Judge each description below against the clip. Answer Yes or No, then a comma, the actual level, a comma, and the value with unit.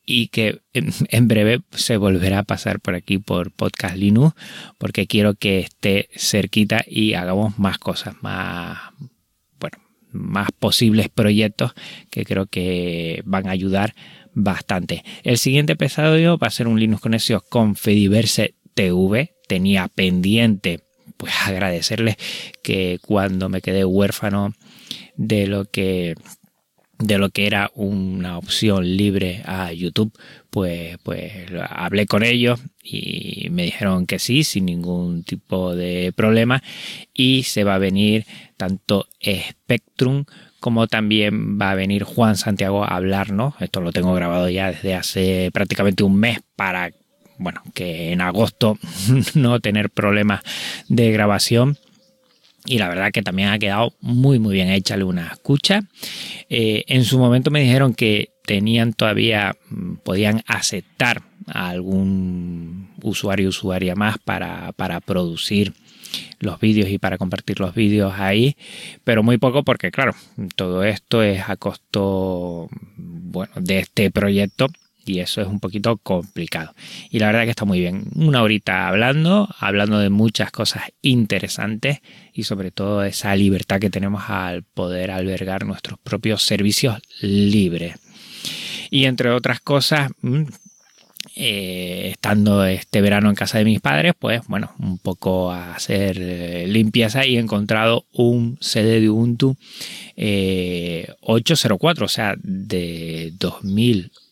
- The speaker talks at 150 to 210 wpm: No, average, 140 wpm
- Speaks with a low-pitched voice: Yes, low, 105 Hz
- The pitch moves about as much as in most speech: Yes, average, 3.4 semitones